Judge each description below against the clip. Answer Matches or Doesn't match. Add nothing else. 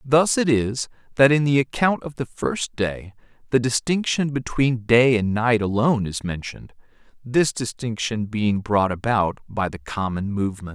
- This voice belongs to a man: Matches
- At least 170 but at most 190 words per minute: Matches